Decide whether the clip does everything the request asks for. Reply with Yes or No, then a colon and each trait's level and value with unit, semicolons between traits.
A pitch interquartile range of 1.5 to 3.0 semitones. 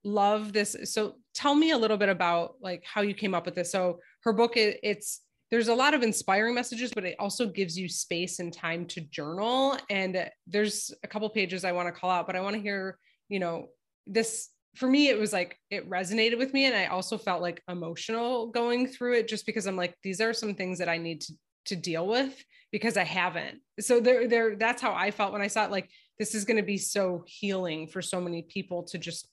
No: average, 4.0 semitones